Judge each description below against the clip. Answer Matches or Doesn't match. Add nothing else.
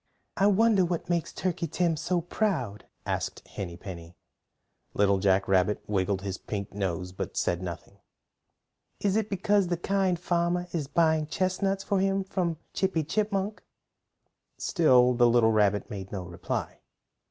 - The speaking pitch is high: Doesn't match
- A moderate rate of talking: Matches